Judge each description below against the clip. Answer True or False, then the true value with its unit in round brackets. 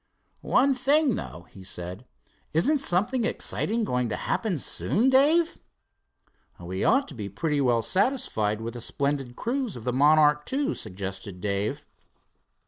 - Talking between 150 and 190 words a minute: False (140 wpm)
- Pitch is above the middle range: False (150 Hz)